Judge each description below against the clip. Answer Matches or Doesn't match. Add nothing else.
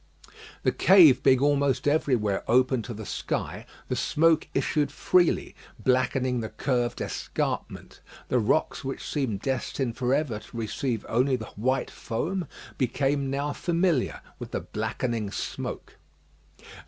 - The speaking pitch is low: Matches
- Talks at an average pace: Doesn't match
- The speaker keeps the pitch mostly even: Doesn't match